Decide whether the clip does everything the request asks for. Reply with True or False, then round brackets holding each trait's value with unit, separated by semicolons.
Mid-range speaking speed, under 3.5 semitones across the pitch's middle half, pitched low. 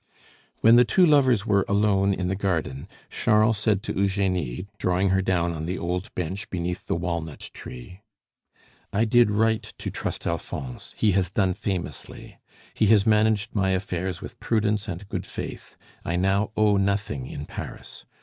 True (165 wpm; 3.1 semitones; 95 Hz)